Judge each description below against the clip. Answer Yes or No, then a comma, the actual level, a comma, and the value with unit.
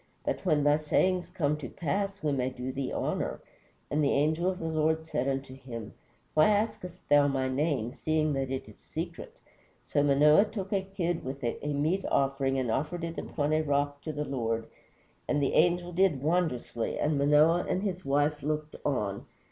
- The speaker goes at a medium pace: Yes, average, 190 wpm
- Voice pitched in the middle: Yes, medium, 150 Hz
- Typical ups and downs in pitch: Yes, average, 3.5 semitones